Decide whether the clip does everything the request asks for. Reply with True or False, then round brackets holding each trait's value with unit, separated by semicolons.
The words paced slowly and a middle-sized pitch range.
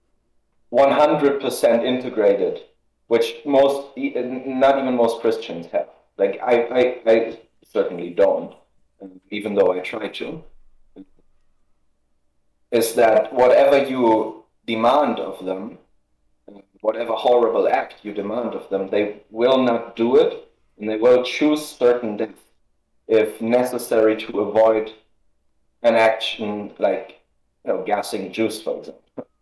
True (120 wpm; 4.1 semitones)